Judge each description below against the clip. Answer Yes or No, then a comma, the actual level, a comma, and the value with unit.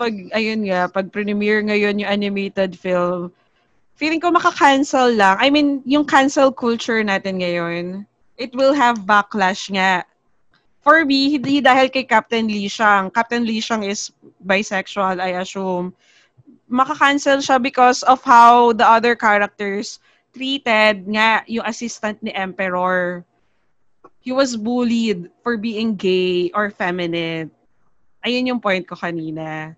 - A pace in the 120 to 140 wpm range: Yes, slow, 135 wpm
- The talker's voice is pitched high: Yes, high, 215 Hz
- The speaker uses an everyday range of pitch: Yes, average, 4.6 semitones